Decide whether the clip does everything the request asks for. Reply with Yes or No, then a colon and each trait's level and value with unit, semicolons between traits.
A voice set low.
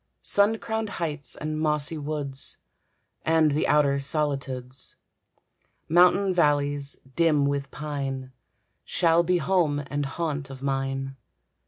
No: medium, 145 Hz